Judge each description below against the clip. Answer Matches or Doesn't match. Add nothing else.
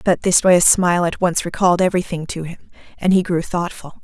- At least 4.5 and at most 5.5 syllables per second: Doesn't match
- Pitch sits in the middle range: Matches